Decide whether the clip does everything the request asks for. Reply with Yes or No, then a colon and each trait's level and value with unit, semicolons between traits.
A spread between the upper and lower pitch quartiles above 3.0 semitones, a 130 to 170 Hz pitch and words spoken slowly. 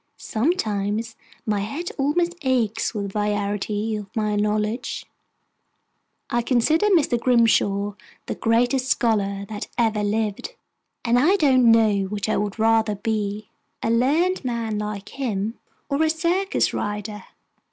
No: average, 3.7 semitones; high, 225 Hz; slow, 130 wpm